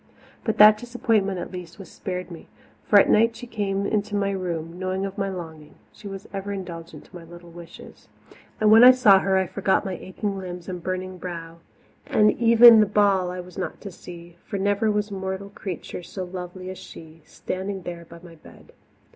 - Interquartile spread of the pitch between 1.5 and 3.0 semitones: Yes, narrow, 2.4 semitones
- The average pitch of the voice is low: No, high, 190 Hz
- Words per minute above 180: Yes, average, 200 wpm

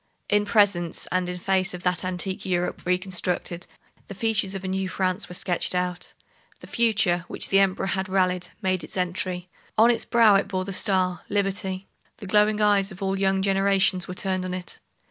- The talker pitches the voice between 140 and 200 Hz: Yes, high, 190 Hz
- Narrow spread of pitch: Yes, narrow, 1.5 semitones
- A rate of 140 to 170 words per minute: No, average, 190 wpm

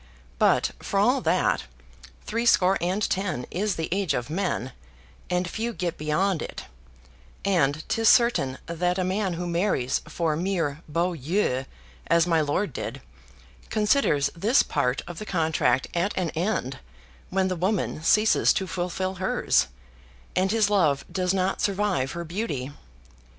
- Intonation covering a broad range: No, average, 3.9 semitones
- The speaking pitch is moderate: Yes, medium, 180 Hz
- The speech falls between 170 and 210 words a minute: No, average, 145 wpm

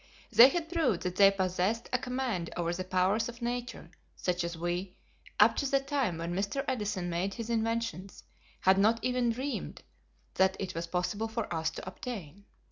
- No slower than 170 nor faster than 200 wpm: Yes, average, 180 wpm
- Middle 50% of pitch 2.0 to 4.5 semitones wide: No, average, 5.0 semitones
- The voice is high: Yes, high, 200 Hz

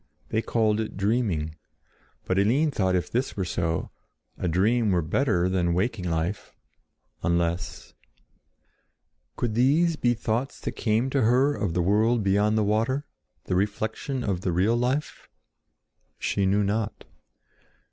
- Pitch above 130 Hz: No, low, 105 Hz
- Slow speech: No, average, 145 wpm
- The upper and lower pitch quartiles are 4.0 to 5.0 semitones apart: Yes, average, 4.7 semitones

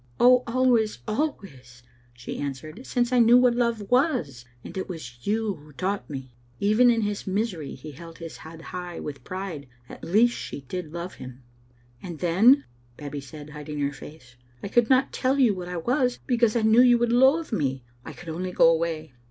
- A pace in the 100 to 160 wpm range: No, average, 195 wpm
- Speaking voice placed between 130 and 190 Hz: Yes, medium, 185 Hz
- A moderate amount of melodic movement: No, wide, 8.0 semitones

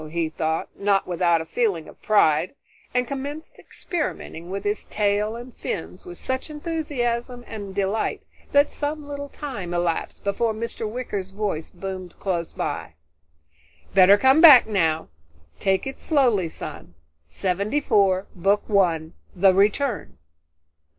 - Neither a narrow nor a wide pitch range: No, wide, 5.8 semitones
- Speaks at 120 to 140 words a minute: Yes, slow, 135 wpm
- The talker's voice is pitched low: No, high, 205 Hz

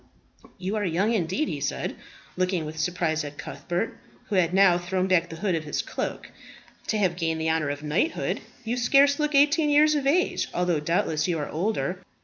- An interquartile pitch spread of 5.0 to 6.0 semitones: Yes, wide, 5.6 semitones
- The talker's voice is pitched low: No, medium, 180 Hz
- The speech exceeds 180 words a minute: Yes, average, 195 wpm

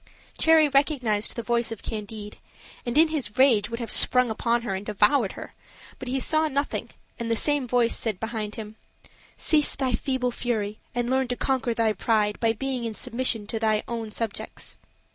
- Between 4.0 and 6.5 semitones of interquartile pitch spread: No, average, 3.2 semitones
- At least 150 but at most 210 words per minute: Yes, average, 185 wpm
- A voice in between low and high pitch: No, high, 235 Hz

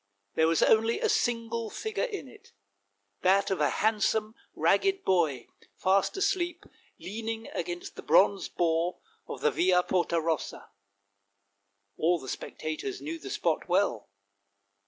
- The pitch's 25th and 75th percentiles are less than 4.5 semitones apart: No, average, 5.3 semitones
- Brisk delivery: No, slow, 135 wpm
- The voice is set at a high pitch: Yes, high, 200 Hz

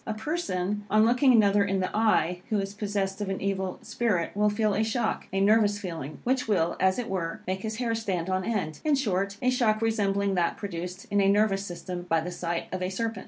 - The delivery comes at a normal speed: No, fast, 225 wpm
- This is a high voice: Yes, high, 200 Hz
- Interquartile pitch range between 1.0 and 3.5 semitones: Yes, average, 2.8 semitones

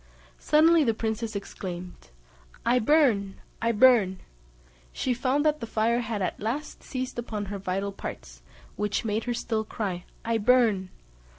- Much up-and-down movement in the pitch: No, average, 3.8 semitones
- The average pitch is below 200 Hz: No, high, 225 Hz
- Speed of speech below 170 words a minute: Yes, average, 150 wpm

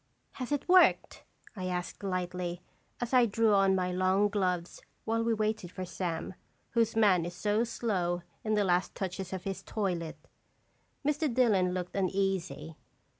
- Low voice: No, high, 190 Hz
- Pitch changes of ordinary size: Yes, average, 3.4 semitones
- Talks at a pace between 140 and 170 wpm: Yes, average, 155 wpm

